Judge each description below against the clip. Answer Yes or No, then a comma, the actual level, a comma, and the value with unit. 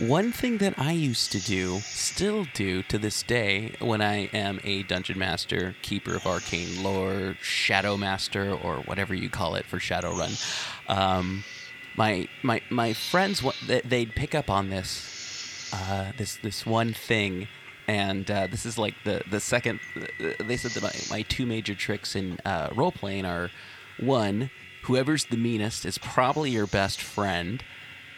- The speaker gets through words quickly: No, average, 160 wpm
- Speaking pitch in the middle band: No, low, 105 Hz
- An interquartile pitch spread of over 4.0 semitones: No, average, 3.5 semitones